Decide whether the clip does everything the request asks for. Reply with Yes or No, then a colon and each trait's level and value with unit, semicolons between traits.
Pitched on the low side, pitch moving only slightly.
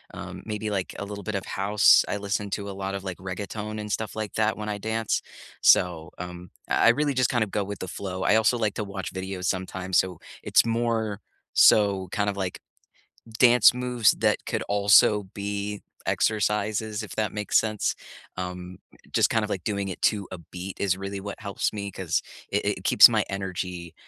Yes: low, 100 Hz; narrow, 2.2 semitones